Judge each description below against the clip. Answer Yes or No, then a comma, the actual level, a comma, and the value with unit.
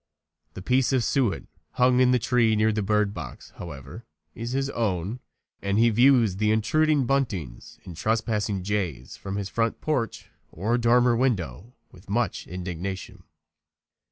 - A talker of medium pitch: No, low, 110 Hz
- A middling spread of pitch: Yes, average, 4.3 semitones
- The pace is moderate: Yes, average, 150 wpm